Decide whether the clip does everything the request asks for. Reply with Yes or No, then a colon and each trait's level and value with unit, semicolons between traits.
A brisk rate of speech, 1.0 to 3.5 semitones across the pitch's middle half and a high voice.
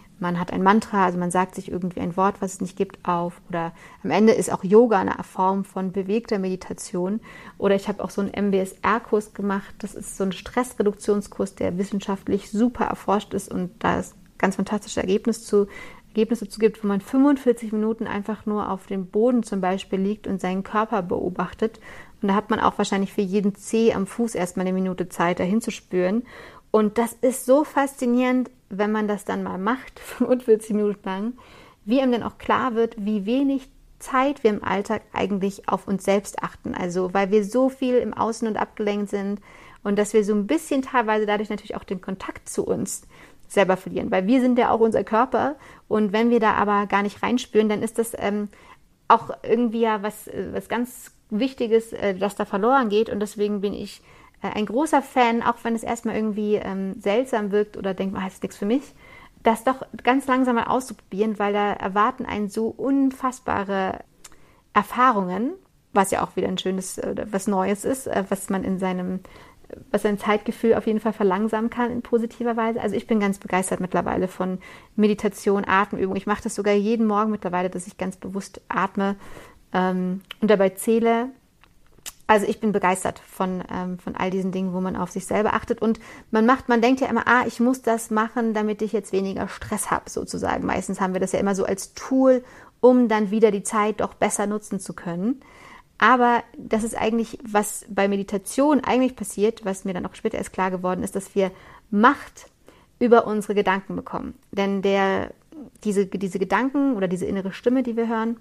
Yes: fast, 195 wpm; average, 2.9 semitones; high, 210 Hz